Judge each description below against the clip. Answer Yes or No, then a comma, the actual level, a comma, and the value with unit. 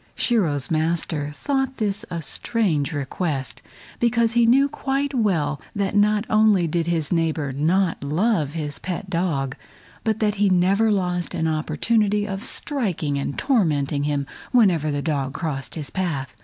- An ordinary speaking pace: Yes, average, 150 wpm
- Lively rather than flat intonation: Yes, wide, 6.2 semitones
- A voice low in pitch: No, medium, 175 Hz